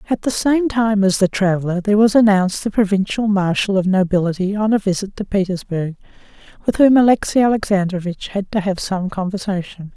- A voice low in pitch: No, high, 200 Hz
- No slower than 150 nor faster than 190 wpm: Yes, average, 175 wpm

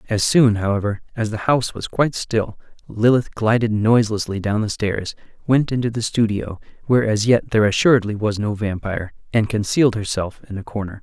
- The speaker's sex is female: No, male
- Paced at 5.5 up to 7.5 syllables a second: Yes, 5.7 syllables/s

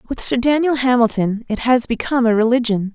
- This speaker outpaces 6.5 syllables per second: No, 5.6 syllables/s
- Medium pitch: No, high, 240 Hz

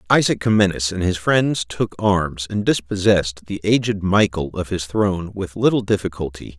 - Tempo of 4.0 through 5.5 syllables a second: Yes, 5.0 syllables/s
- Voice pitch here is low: Yes, very low, 95 Hz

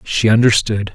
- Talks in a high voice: No, low, 110 Hz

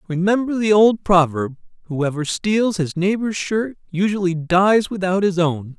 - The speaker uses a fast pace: No, average, 145 wpm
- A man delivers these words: Yes, male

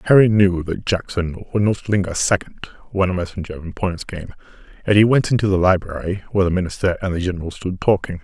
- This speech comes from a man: Yes, male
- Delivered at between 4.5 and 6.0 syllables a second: No, 7.0 syllables/s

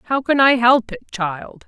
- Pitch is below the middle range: No, high, 235 Hz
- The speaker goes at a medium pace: No, fast, 215 wpm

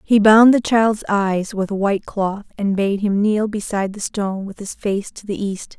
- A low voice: No, high, 205 Hz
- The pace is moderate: No, fast, 230 wpm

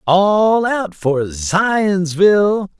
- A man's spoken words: Yes, male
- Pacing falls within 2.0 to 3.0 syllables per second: Yes, 2.3 syllables/s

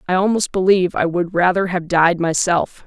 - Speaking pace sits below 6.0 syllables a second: Yes, 5.2 syllables/s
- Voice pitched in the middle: Yes, medium, 180 Hz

